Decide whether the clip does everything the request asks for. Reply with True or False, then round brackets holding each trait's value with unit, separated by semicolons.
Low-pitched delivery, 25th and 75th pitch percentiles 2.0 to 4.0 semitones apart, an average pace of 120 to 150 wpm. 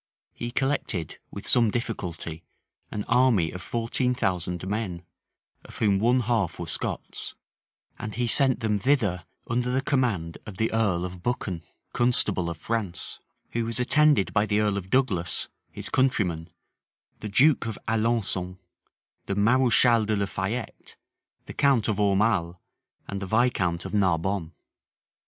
False (105 Hz; 4.6 semitones; 145 wpm)